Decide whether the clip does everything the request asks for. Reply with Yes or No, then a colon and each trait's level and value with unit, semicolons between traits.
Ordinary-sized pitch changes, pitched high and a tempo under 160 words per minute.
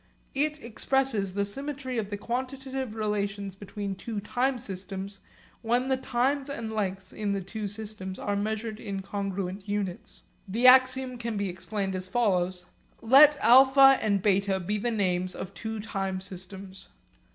Yes: average, 4.2 semitones; high, 210 Hz; average, 150 wpm